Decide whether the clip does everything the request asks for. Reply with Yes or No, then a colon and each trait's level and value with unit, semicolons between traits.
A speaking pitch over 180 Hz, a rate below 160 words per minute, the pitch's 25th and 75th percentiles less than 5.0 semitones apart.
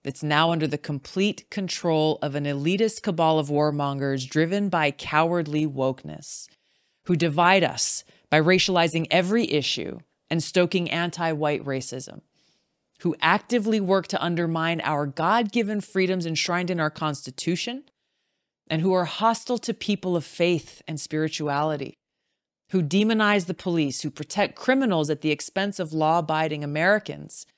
No: medium, 165 Hz; average, 140 wpm; average, 3.9 semitones